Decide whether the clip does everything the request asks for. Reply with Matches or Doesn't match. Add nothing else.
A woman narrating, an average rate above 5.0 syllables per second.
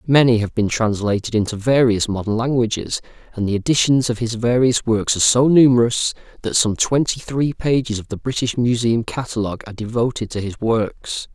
Doesn't match